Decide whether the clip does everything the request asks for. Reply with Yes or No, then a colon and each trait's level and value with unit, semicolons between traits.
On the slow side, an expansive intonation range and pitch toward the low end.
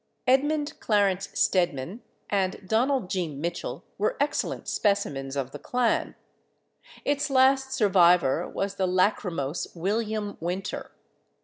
No: slow, 110 wpm; wide, 5.8 semitones; high, 200 Hz